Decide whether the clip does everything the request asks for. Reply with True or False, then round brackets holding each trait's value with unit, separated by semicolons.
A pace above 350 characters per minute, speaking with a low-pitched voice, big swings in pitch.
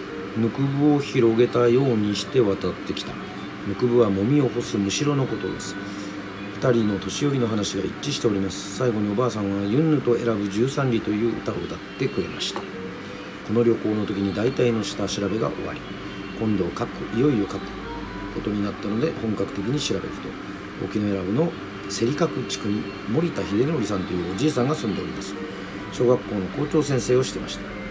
False (375 characters per minute; 105 Hz; 3.6 semitones)